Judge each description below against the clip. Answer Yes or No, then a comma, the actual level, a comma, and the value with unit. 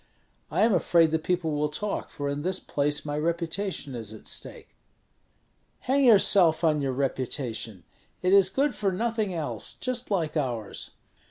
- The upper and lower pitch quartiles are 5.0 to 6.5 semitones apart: Yes, wide, 5.5 semitones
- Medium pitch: Yes, medium, 160 Hz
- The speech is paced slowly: No, average, 160 wpm